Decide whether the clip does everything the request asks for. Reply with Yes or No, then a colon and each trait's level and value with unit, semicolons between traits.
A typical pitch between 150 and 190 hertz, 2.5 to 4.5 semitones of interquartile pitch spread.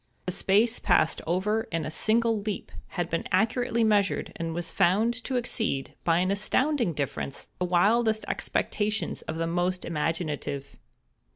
No: medium, 185 Hz; average, 4.9 semitones